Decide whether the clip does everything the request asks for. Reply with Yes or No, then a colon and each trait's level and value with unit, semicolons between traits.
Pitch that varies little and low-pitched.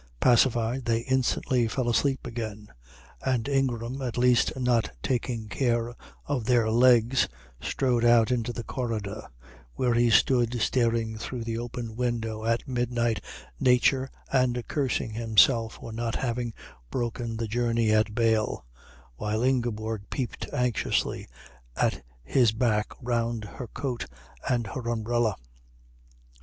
Yes: narrow, 1.8 semitones; low, 120 Hz